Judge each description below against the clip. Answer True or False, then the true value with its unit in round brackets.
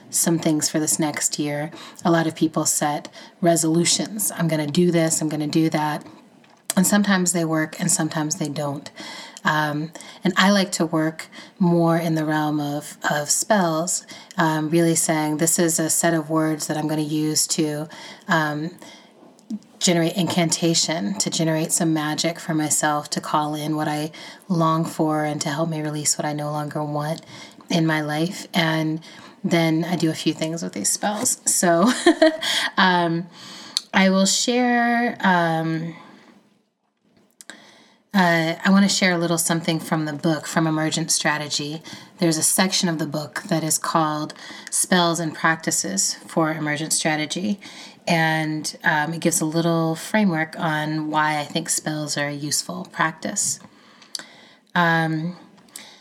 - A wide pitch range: False (2.7 semitones)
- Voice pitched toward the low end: False (165 Hz)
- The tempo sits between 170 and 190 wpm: False (160 wpm)